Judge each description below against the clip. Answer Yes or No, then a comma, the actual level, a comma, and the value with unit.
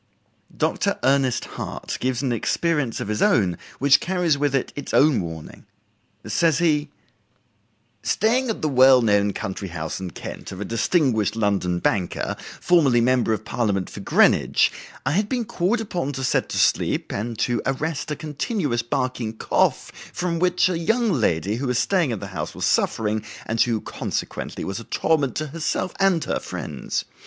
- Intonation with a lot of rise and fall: Yes, wide, 7.1 semitones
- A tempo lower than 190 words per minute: Yes, average, 170 wpm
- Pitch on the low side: Yes, low, 130 Hz